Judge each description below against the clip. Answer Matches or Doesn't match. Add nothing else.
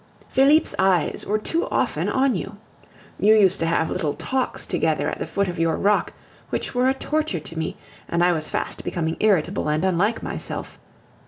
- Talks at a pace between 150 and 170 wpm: Doesn't match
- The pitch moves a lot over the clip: Matches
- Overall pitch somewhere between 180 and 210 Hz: Matches